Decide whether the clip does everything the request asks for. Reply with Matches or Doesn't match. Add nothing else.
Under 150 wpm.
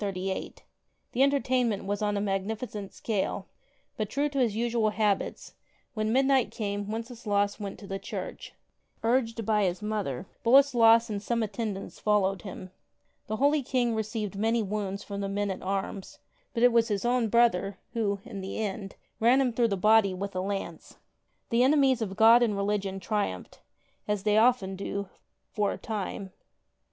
Doesn't match